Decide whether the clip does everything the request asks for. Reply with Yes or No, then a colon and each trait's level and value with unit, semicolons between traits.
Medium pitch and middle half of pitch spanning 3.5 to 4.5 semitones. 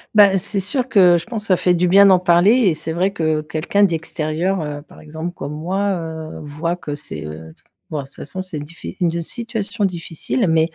Yes: medium, 170 Hz; average, 3.8 semitones